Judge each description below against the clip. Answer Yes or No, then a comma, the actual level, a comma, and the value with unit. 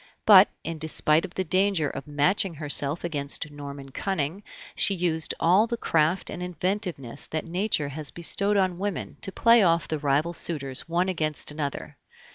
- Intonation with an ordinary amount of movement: Yes, average, 4.1 semitones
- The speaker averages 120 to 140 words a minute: No, average, 165 wpm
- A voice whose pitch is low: No, medium, 165 Hz